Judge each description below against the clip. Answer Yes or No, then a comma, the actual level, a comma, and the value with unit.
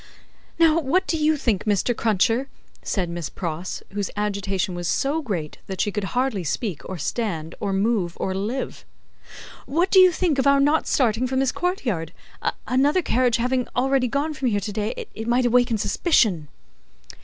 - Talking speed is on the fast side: No, average, 175 wpm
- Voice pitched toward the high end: Yes, high, 235 Hz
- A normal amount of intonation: No, wide, 5.8 semitones